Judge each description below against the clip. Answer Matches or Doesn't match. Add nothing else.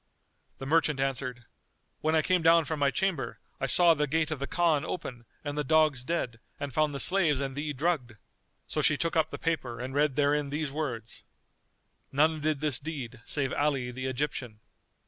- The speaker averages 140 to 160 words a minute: Doesn't match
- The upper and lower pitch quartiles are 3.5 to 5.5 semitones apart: Doesn't match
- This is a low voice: Doesn't match